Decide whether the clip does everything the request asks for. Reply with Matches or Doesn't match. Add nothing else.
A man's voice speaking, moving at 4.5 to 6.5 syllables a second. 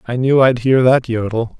Matches